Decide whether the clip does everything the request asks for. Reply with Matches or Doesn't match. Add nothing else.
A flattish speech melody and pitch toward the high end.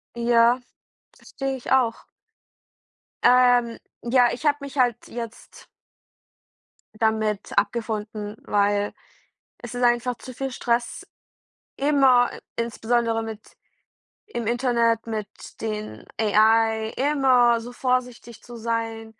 Matches